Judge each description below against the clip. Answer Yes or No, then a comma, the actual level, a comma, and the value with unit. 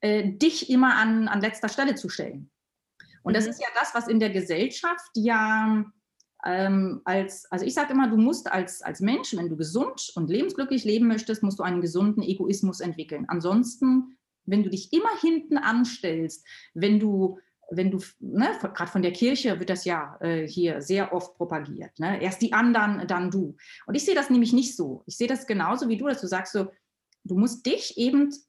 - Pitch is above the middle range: Yes, high, 210 Hz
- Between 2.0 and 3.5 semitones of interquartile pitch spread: No, average, 4.8 semitones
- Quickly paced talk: Yes, fast, 200 wpm